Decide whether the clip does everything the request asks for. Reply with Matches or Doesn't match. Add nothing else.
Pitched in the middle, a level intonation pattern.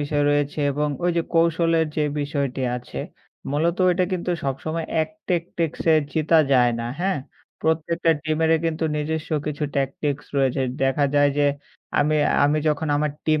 Matches